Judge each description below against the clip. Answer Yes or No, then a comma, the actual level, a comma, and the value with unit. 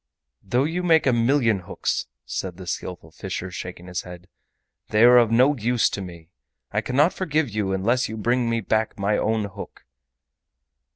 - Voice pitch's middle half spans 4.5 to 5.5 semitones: Yes, average, 4.8 semitones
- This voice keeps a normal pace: Yes, average, 175 wpm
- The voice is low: Yes, low, 110 Hz